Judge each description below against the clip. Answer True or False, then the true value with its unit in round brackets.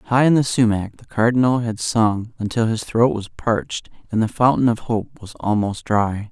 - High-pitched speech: False (115 Hz)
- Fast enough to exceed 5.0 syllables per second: False (4.8 syllables/s)